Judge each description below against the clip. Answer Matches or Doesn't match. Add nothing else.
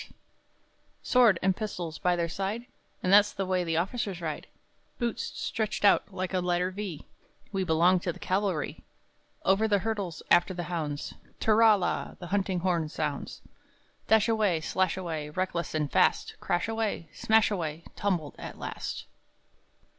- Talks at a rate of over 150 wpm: Doesn't match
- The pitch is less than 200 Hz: Matches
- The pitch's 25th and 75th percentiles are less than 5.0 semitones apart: Matches